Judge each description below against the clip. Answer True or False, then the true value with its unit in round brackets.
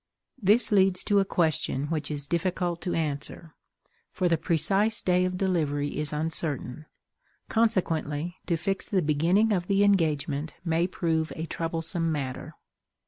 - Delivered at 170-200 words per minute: False (140 wpm)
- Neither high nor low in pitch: True (165 Hz)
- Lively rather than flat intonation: False (3.4 semitones)